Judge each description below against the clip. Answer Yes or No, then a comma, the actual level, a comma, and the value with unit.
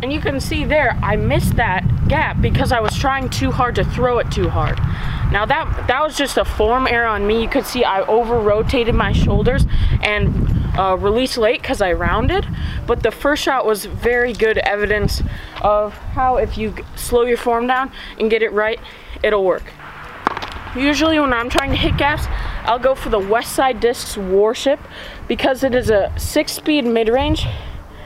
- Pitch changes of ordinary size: Yes, average, 3.6 semitones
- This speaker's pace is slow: No, average, 190 wpm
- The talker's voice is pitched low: No, high, 235 Hz